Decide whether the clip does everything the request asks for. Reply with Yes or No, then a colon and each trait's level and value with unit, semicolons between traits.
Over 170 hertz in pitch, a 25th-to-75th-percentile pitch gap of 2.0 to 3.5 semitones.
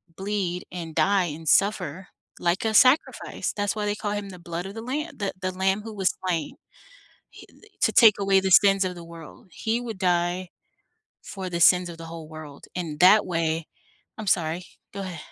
Yes: medium, 185 Hz; average, 3.1 semitones